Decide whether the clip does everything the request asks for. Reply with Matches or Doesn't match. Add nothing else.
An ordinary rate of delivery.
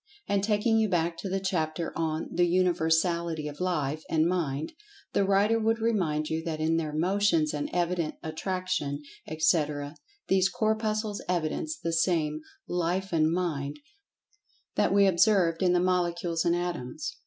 Matches